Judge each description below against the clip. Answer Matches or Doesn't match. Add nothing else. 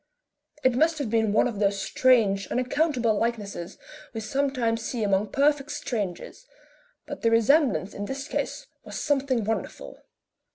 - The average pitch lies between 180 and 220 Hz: Doesn't match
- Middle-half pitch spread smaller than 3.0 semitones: Doesn't match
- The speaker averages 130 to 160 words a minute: Matches